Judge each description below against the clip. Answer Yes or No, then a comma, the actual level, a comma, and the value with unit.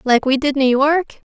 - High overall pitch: Yes, very high, 275 Hz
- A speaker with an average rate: No, fast, 230 wpm